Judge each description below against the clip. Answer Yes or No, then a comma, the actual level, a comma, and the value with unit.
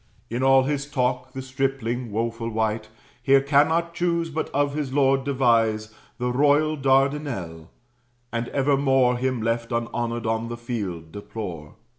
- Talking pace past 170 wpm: No, average, 140 wpm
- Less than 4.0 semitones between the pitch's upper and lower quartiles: Yes, average, 3.2 semitones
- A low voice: Yes, low, 125 Hz